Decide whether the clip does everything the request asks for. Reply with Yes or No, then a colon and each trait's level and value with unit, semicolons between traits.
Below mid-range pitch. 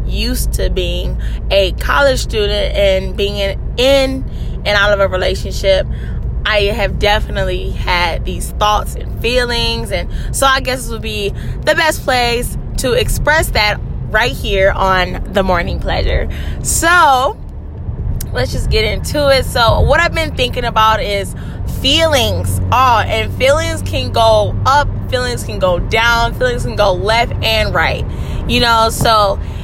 No: high, 190 Hz